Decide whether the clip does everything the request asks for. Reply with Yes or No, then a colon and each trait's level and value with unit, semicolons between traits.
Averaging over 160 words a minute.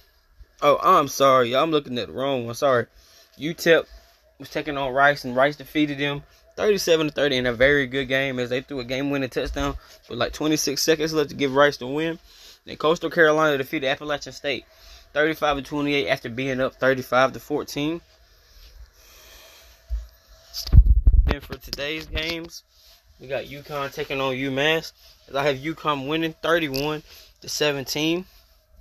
No: average, 145 wpm